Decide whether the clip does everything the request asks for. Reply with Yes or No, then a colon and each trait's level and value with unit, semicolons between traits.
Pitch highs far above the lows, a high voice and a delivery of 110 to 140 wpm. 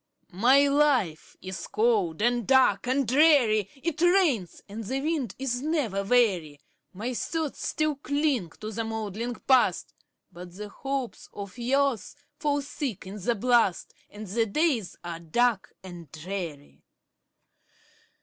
Yes: wide, 6.0 semitones; high, 235 Hz; slow, 135 wpm